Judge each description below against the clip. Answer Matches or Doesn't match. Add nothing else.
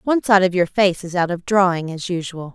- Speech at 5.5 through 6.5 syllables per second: Matches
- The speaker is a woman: Matches